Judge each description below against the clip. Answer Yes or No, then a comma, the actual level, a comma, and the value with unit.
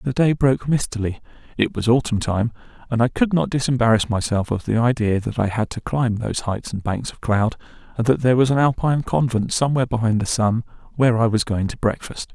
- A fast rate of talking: Yes, fast, 220 wpm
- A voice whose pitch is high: No, low, 120 Hz